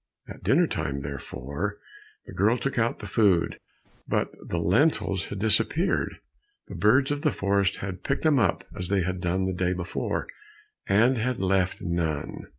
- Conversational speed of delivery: Yes, average, 165 wpm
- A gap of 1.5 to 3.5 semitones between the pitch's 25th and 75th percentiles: No, average, 4.3 semitones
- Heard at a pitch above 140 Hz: No, very low, 95 Hz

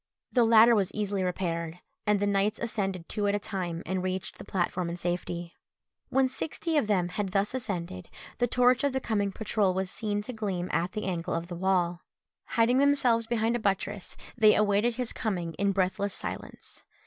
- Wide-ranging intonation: No, average, 3.7 semitones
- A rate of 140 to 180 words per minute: No, average, 190 wpm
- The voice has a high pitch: Yes, high, 200 Hz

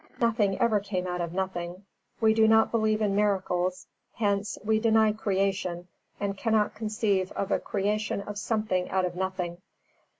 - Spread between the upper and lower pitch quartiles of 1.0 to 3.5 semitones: Yes, narrow, 2.6 semitones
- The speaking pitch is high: Yes, high, 200 Hz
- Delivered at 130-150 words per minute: No, average, 160 wpm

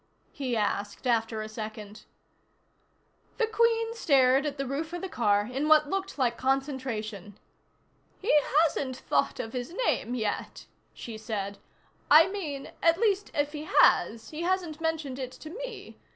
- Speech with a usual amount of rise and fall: No, wide, 6.4 semitones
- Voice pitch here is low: No, very high, 275 Hz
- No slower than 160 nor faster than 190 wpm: No, average, 150 wpm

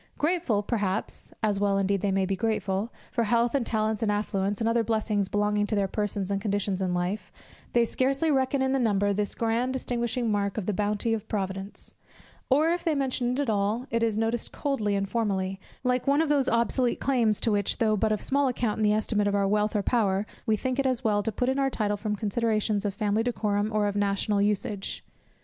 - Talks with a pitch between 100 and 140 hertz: No, high, 215 Hz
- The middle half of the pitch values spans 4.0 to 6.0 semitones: No, average, 2.9 semitones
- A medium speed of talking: No, fast, 220 wpm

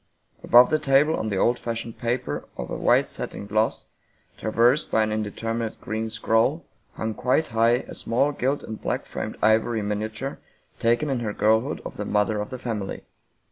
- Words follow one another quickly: No, average, 180 wpm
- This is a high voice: No, low, 115 Hz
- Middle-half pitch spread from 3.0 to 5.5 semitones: No, narrow, 2.4 semitones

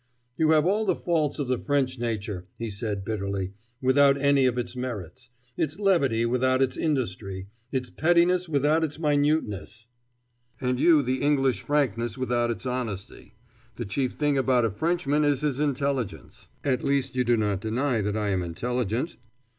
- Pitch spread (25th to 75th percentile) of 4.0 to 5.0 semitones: Yes, average, 4.4 semitones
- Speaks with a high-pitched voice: No, low, 130 Hz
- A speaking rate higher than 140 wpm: Yes, average, 170 wpm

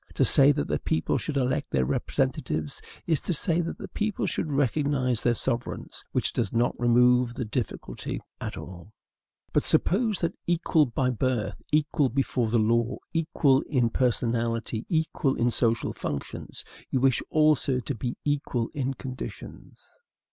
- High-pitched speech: No, low, 125 Hz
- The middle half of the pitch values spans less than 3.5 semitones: No, average, 3.8 semitones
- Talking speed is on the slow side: No, average, 155 wpm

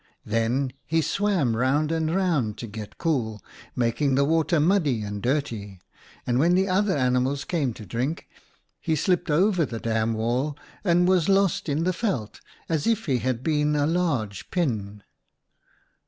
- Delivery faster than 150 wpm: Yes, average, 160 wpm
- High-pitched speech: No, medium, 145 Hz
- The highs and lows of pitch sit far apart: Yes, wide, 6.5 semitones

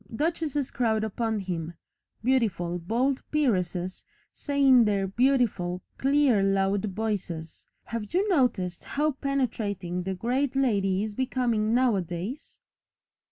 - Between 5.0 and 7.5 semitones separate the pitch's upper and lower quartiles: Yes, wide, 5.5 semitones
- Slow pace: Yes, slow, 115 wpm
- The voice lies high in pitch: Yes, high, 220 Hz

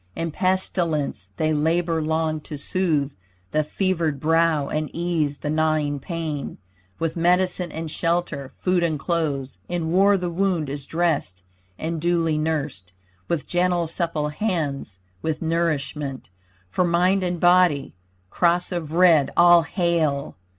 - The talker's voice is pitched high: No, medium, 165 Hz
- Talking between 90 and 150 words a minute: Yes, slow, 135 wpm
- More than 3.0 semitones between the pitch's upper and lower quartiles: No, average, 2.7 semitones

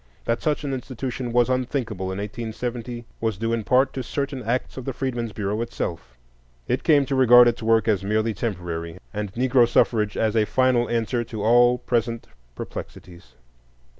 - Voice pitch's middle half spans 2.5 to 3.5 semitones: Yes, average, 2.8 semitones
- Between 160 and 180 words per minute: Yes, average, 170 wpm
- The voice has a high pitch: No, low, 115 Hz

